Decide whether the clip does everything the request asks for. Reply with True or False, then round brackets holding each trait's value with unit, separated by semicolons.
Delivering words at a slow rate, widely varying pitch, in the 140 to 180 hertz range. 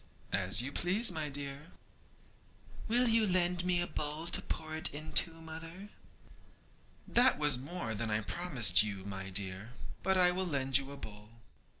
False (165 wpm; 7.5 semitones; 150 Hz)